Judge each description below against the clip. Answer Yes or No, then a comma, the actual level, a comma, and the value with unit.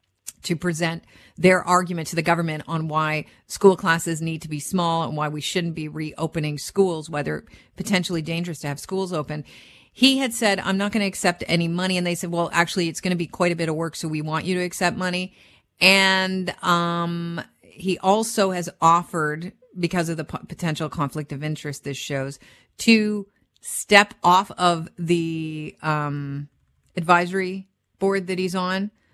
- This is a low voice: No, medium, 170 Hz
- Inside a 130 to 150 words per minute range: No, average, 180 wpm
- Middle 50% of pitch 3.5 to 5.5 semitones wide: No, average, 3.0 semitones